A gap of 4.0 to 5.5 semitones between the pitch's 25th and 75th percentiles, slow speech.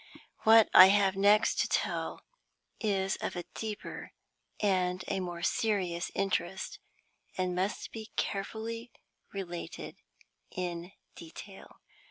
No: average, 2.7 semitones; slow, 110 wpm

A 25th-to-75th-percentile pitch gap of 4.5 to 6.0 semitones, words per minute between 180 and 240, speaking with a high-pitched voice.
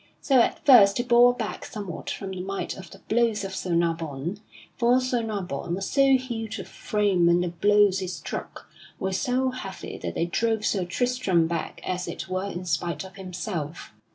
Yes: average, 4.9 semitones; average, 190 wpm; high, 195 Hz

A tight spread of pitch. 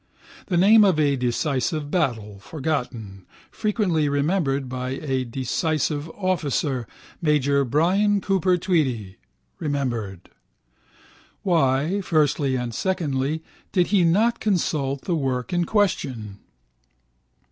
No: wide, 5.4 semitones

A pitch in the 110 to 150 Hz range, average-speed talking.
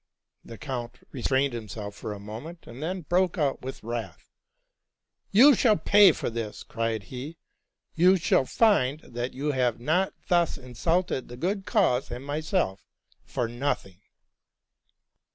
Yes: low, 135 Hz; average, 150 wpm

